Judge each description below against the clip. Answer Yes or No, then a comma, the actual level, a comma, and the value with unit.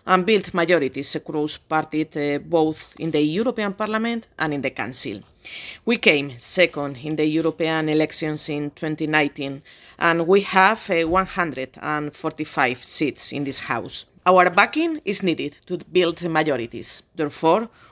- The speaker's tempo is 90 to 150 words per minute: Yes, slow, 135 wpm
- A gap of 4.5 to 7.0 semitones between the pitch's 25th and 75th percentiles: No, average, 3.5 semitones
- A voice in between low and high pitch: Yes, medium, 160 Hz